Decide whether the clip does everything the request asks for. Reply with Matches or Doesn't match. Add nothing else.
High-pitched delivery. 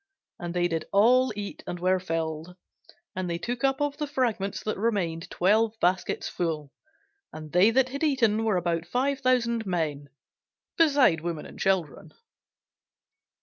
Matches